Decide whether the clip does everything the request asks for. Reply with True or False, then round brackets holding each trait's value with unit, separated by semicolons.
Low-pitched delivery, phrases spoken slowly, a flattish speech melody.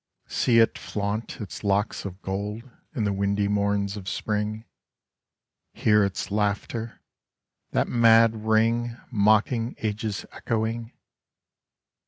True (105 Hz; 120 wpm; 1.9 semitones)